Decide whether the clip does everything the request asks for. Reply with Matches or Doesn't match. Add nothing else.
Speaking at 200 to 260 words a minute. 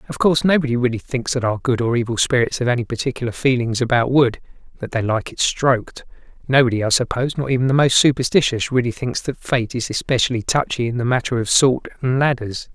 Matches